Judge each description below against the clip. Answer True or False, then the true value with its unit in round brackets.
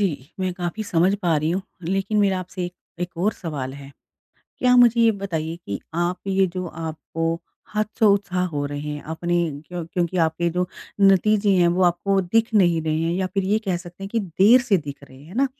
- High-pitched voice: False (180 Hz)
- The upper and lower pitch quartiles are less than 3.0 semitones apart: False (3.3 semitones)